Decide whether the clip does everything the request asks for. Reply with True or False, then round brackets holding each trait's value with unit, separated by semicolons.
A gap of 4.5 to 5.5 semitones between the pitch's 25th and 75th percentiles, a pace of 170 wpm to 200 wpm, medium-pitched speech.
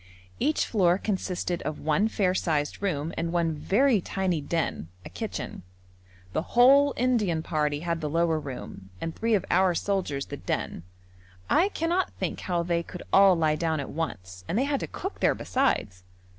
True (5.1 semitones; 175 wpm; 175 Hz)